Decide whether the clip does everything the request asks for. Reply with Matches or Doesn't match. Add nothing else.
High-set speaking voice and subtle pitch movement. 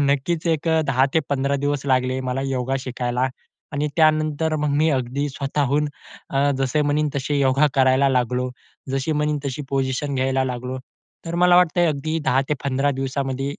Doesn't match